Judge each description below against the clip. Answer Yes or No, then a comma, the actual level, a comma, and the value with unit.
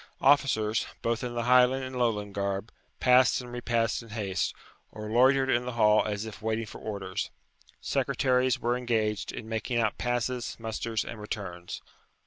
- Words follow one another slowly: No, average, 160 wpm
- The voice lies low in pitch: Yes, low, 115 Hz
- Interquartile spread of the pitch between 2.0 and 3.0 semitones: Yes, narrow, 2.6 semitones